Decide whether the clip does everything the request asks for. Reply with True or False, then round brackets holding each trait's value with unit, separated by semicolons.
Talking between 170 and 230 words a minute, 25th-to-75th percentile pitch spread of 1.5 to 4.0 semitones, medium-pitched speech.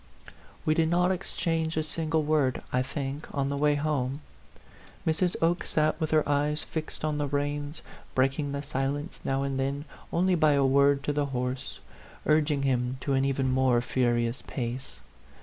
True (175 wpm; 2.5 semitones; 145 Hz)